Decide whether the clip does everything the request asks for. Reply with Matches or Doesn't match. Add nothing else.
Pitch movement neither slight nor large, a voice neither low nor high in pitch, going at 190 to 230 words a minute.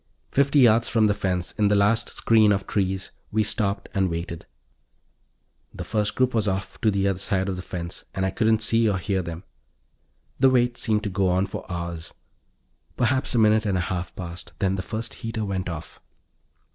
Doesn't match